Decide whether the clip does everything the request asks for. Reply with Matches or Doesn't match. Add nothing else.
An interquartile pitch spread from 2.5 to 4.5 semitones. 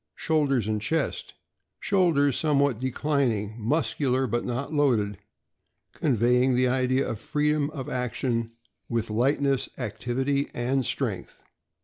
Matches